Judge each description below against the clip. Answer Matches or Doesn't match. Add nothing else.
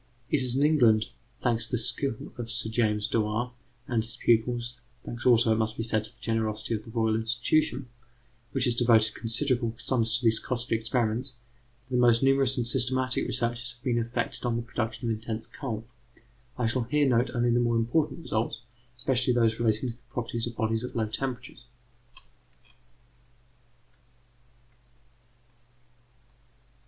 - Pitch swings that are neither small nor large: Doesn't match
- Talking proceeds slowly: Doesn't match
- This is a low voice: Matches